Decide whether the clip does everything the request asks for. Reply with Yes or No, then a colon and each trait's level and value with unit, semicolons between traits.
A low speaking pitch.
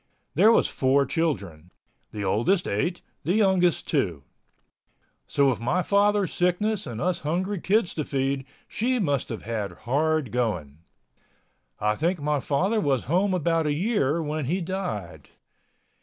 No: medium, 155 Hz